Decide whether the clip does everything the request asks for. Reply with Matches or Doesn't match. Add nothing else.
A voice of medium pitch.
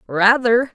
Doesn't match